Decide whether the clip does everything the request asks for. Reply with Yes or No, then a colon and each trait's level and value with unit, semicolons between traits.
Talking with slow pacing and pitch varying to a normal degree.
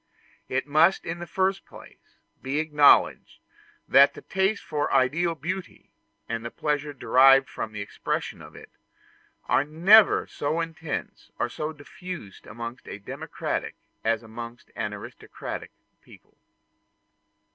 No: slow, 130 wpm; wide, 5.9 semitones